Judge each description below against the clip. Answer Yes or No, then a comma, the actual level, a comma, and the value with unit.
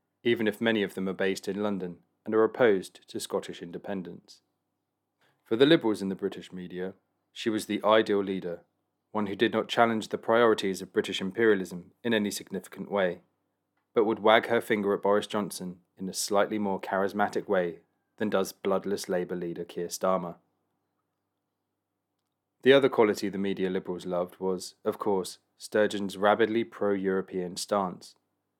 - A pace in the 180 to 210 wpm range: No, average, 160 wpm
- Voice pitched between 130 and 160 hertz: No, low, 100 Hz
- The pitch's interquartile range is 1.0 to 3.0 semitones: Yes, narrow, 2.4 semitones